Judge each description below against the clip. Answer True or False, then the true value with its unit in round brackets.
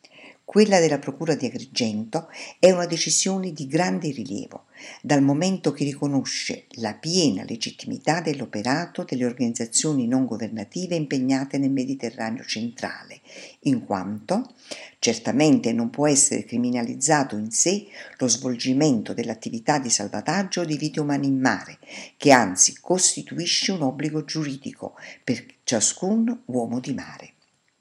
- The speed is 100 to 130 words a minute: True (125 wpm)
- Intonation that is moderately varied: False (6.0 semitones)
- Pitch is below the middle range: False (145 Hz)